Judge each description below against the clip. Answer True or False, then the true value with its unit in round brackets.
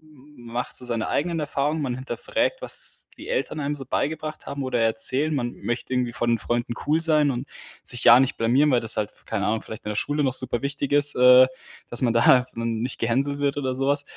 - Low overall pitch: True (130 Hz)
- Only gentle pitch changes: False (3.4 semitones)